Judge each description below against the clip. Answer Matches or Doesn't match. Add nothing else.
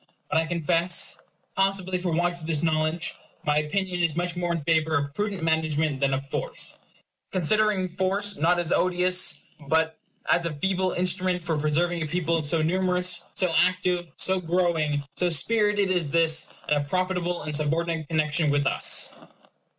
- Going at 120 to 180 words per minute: Matches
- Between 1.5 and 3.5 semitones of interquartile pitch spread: Matches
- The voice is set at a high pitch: Doesn't match